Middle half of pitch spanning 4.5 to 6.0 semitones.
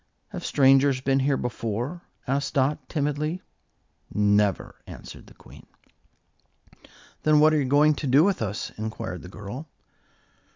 Yes: average, 5.1 semitones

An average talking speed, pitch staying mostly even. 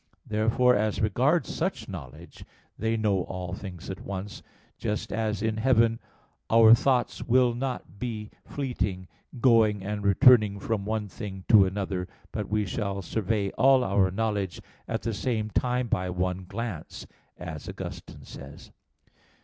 No: average, 150 wpm; average, 3.0 semitones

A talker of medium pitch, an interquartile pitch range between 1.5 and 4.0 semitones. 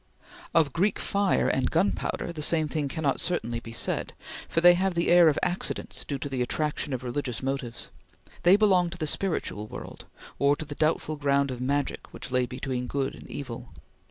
No: medium, 145 Hz; average, 4.7 semitones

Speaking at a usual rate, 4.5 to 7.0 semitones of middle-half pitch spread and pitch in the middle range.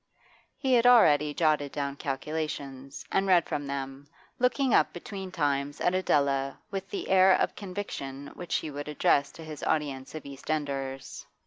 Yes: average, 160 wpm; average, 4.9 semitones; medium, 150 Hz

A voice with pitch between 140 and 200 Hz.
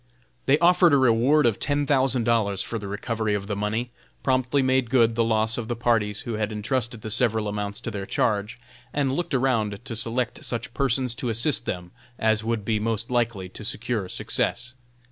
No: low, 115 Hz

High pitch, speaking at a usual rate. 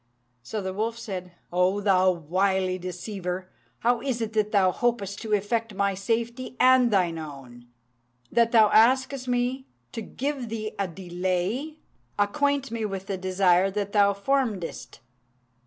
Yes: high, 205 Hz; average, 145 wpm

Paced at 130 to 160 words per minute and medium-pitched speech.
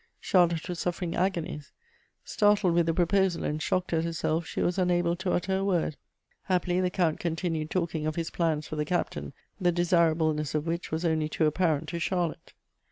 No: average, 185 wpm; medium, 170 Hz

